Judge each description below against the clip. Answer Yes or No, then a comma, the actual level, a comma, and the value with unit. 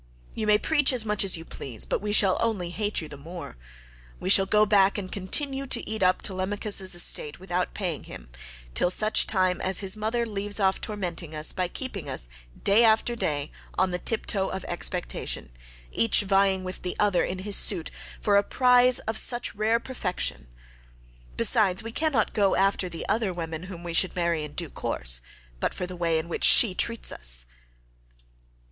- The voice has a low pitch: No, high, 190 Hz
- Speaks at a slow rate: No, average, 190 wpm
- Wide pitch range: No, average, 3.5 semitones